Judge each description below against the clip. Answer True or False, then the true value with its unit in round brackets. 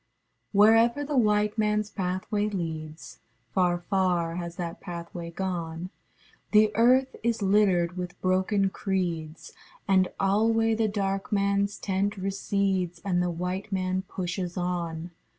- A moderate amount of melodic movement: True (3.0 semitones)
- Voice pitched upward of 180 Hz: True (190 Hz)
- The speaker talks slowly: True (125 wpm)